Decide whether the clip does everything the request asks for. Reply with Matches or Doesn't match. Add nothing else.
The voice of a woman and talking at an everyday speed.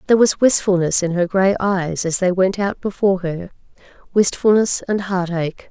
Matches